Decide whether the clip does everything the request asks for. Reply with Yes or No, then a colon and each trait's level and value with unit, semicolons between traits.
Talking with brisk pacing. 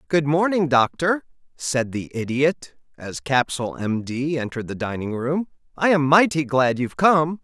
No: average, 160 wpm